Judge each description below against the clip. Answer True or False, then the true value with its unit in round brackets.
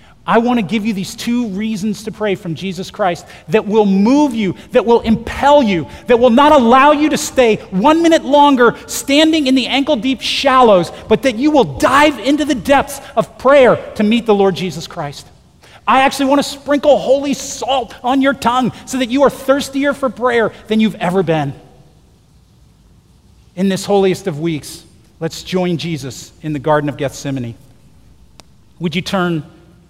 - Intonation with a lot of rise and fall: True (7.1 semitones)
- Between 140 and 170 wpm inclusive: False (180 wpm)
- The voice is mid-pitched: False (225 Hz)